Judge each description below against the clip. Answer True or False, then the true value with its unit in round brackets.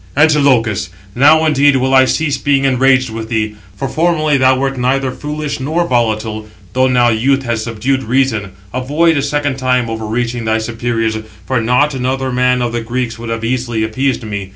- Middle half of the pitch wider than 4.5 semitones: False (3.2 semitones)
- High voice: False (130 Hz)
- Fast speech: False (175 wpm)